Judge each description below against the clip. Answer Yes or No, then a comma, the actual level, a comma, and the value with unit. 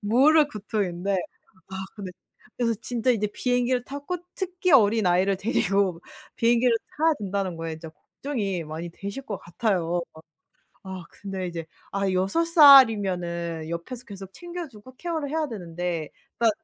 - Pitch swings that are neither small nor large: No, wide, 6.0 semitones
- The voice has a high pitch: Yes, high, 205 Hz